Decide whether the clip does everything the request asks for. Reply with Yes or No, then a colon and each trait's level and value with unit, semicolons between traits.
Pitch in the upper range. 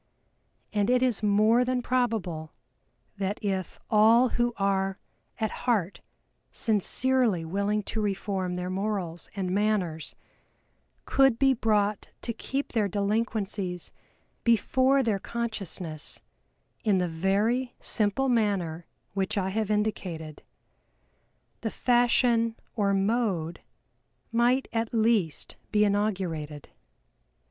Yes: high, 210 Hz